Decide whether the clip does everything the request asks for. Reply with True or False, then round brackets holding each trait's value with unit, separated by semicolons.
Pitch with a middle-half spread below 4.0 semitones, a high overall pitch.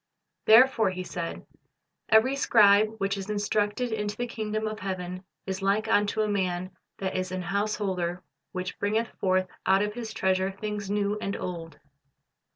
True (2.5 semitones; 200 Hz)